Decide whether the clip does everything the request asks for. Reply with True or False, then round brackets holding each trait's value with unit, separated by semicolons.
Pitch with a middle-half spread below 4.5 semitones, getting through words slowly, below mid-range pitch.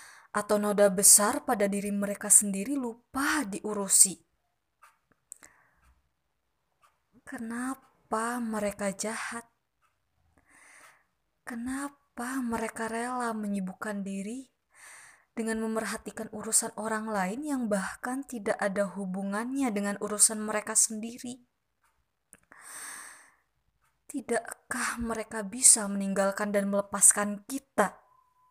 False (3.0 semitones; 80 wpm; 220 Hz)